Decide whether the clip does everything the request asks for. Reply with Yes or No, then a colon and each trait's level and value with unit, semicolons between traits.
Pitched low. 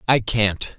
Yes: low, 110 Hz